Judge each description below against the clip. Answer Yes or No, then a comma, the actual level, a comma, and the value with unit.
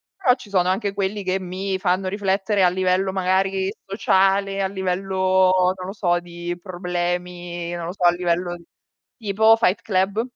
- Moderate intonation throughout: No, narrow, 1.6 semitones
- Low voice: No, high, 190 Hz